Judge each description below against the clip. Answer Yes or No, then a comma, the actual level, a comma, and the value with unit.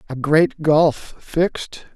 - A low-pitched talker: No, medium, 155 Hz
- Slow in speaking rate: Yes, slow, 125 wpm